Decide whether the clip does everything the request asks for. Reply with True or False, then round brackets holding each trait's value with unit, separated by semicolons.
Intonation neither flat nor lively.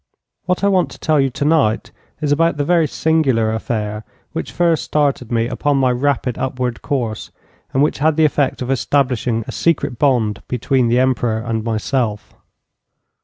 True (4.1 semitones)